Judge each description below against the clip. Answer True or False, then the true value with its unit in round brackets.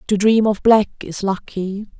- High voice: True (205 Hz)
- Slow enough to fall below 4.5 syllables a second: True (4.1 syllables/s)